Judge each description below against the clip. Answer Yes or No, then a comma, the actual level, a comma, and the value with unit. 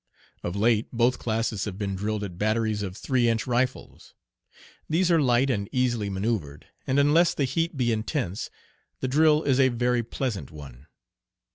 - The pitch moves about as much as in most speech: Yes, average, 4.3 semitones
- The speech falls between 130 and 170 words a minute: Yes, average, 165 wpm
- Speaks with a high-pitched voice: No, low, 115 Hz